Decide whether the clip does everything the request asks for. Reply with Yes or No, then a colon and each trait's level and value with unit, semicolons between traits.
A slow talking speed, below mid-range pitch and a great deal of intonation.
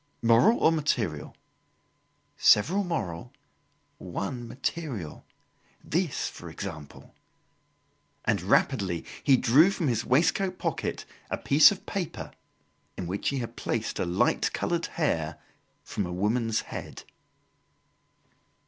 Yes: slow, 110 wpm; low, 120 Hz; wide, 8.4 semitones